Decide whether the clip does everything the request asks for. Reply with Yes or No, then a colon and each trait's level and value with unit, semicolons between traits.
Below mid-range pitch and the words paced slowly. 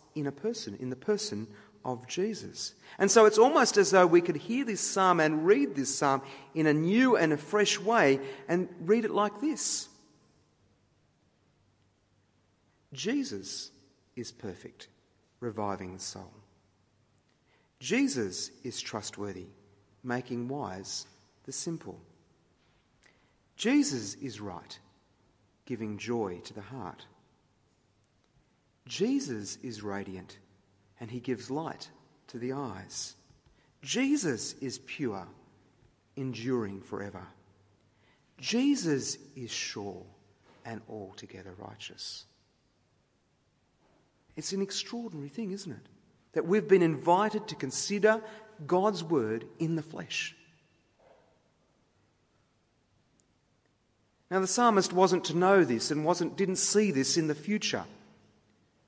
Yes: low, 130 Hz; slow, 110 wpm